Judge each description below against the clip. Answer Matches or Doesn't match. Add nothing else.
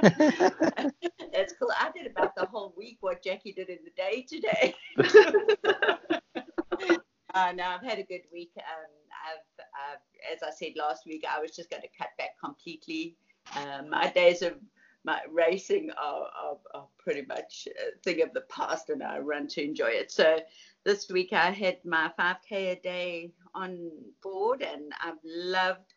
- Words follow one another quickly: Doesn't match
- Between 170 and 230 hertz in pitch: Matches